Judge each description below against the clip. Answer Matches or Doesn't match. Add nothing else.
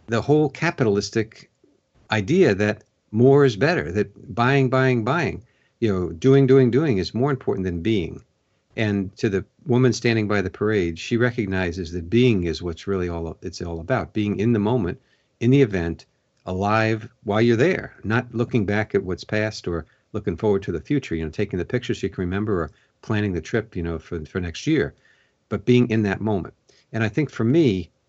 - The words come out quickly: Doesn't match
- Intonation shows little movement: Doesn't match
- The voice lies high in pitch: Doesn't match